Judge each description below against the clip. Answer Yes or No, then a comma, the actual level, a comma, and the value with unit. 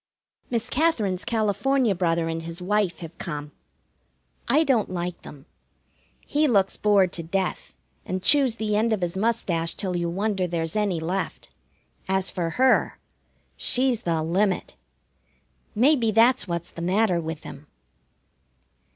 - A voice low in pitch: No, high, 190 Hz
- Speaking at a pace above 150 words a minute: No, average, 140 wpm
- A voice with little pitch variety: No, average, 4.7 semitones